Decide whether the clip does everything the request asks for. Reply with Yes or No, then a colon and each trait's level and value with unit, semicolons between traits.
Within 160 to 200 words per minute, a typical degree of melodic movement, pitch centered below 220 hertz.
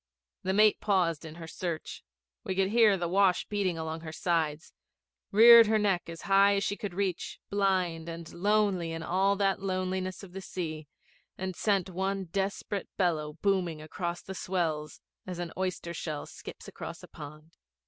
Yes: average, 170 wpm; average, 3.0 semitones; medium, 185 Hz